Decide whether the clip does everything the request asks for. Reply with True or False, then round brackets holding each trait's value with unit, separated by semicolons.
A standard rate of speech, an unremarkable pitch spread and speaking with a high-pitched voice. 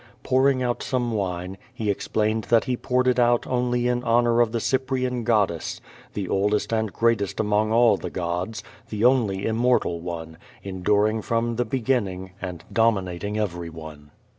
False (155 wpm; 4.1 semitones; 110 Hz)